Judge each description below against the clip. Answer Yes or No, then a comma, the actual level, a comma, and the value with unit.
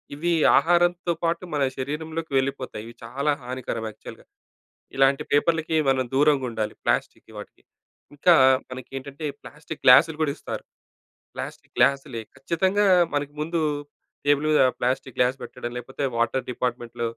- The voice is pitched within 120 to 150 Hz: Yes, medium, 140 Hz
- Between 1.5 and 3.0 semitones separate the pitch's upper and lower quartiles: No, average, 3.8 semitones